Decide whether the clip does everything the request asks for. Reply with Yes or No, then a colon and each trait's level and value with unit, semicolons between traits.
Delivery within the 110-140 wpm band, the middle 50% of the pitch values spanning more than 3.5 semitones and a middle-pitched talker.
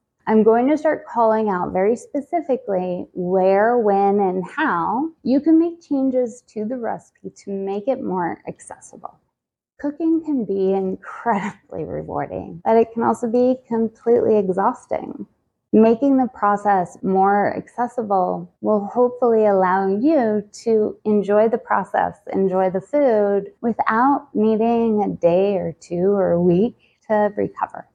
No: slow, 135 wpm; average, 4.1 semitones; high, 220 Hz